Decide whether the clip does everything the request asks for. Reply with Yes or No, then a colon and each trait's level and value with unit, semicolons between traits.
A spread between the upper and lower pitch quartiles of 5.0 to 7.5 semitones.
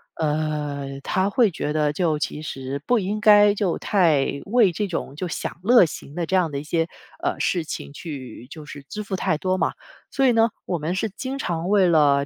Yes: average, 5.3 semitones